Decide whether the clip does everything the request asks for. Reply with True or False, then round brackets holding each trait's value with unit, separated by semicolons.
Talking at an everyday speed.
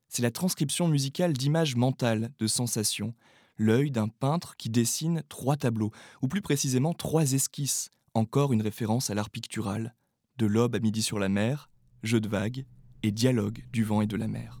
True (180 wpm)